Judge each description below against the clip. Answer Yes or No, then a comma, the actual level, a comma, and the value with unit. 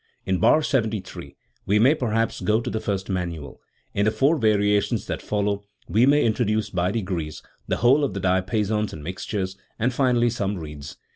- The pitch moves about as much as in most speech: Yes, average, 3.6 semitones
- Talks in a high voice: No, low, 105 Hz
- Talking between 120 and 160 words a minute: No, average, 175 wpm